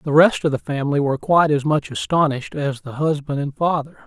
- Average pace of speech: No, fast, 220 wpm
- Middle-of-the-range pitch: Yes, medium, 145 Hz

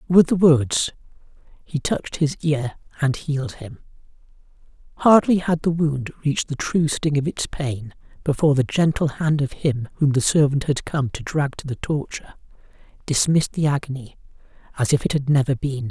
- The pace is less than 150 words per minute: No, average, 175 wpm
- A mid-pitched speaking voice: Yes, medium, 145 Hz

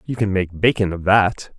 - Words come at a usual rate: No, fast, 230 wpm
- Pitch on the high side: No, low, 100 Hz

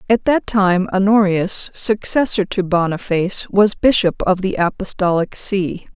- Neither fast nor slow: No, slow, 130 wpm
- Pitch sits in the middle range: No, high, 195 Hz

